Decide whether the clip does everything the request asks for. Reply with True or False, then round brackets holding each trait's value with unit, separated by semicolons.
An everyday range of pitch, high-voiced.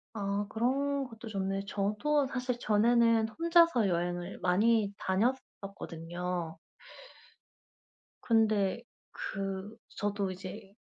True (3.6 semitones; 205 Hz)